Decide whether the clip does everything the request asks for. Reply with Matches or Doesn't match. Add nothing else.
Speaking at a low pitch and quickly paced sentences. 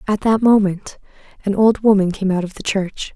Doesn't match